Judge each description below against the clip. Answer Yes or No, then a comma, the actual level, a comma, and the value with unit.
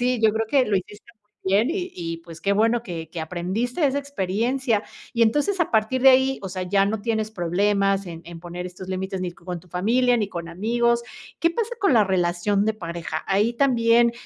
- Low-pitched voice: No, high, 210 Hz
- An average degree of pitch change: Yes, average, 4.8 semitones